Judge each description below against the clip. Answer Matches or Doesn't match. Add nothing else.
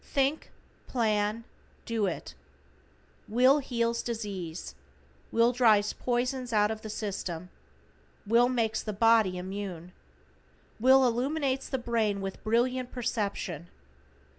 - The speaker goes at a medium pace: Doesn't match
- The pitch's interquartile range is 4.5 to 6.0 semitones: Doesn't match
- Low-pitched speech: Doesn't match